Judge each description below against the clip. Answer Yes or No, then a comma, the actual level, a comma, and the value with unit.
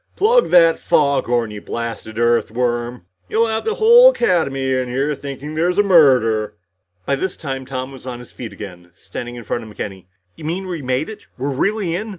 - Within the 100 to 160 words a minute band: No, average, 190 wpm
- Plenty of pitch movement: Yes, wide, 6.6 semitones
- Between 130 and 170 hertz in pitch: Yes, low, 135 Hz